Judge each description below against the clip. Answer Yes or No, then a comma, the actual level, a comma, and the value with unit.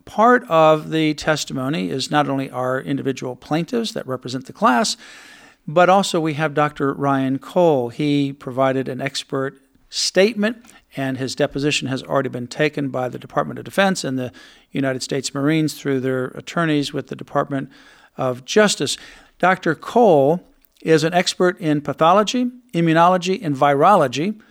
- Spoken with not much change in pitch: No, average, 4.5 semitones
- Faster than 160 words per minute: No, average, 150 wpm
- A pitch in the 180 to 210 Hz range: No, medium, 145 Hz